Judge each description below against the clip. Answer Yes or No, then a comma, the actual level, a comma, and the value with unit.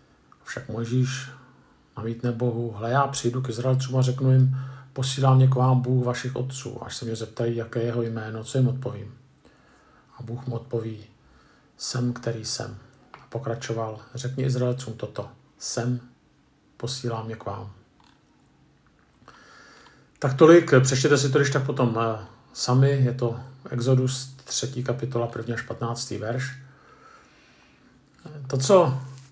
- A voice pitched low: Yes, low, 125 Hz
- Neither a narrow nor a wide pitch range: No, narrow, 2.2 semitones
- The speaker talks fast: No, average, 140 wpm